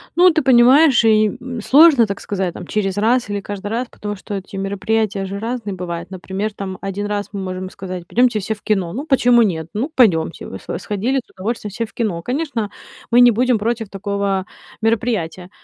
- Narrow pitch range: No, average, 3.7 semitones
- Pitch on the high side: Yes, high, 210 Hz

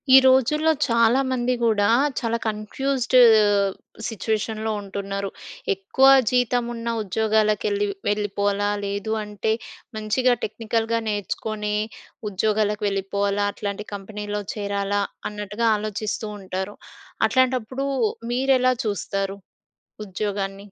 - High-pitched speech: Yes, high, 210 Hz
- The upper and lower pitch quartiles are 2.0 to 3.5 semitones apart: Yes, narrow, 2.4 semitones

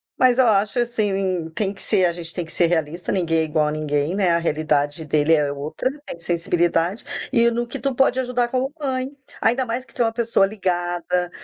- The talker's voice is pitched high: No, medium, 180 Hz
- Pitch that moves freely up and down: Yes, wide, 6.3 semitones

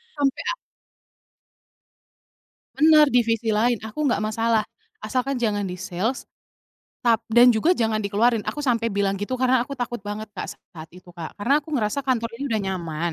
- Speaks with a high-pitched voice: Yes, high, 230 Hz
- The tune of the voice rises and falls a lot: No, average, 3.6 semitones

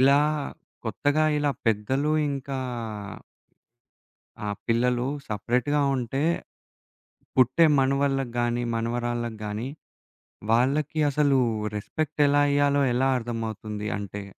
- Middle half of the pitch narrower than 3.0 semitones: No, average, 3.5 semitones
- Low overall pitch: Yes, low, 125 Hz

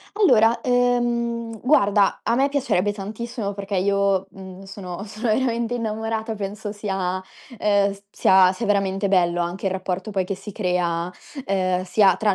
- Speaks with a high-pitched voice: Yes, high, 200 Hz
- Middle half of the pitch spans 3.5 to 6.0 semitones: No, average, 2.9 semitones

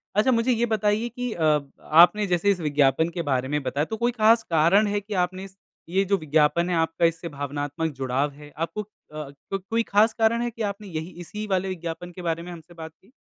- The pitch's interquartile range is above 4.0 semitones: Yes, average, 5.0 semitones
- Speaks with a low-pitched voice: No, medium, 175 Hz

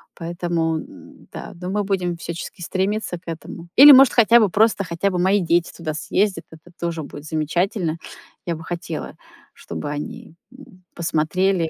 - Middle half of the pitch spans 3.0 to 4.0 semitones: Yes, average, 3.3 semitones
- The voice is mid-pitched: Yes, medium, 175 Hz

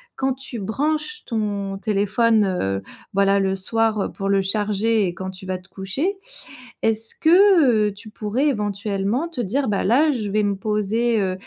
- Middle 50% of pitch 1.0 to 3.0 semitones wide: No, average, 3.5 semitones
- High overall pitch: Yes, high, 210 Hz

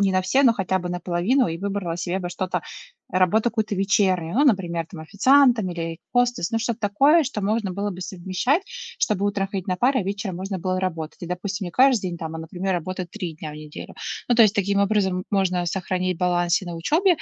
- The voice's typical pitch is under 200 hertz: Yes, high, 190 Hz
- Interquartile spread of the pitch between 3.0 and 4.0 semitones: Yes, average, 3.3 semitones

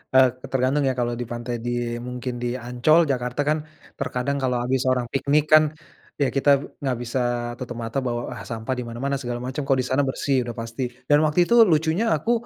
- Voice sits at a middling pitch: No, low, 130 Hz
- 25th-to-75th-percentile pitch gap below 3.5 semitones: Yes, narrow, 2.6 semitones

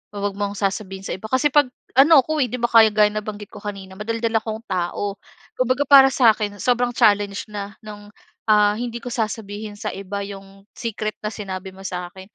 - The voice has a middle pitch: No, high, 210 Hz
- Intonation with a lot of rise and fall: No, average, 2.8 semitones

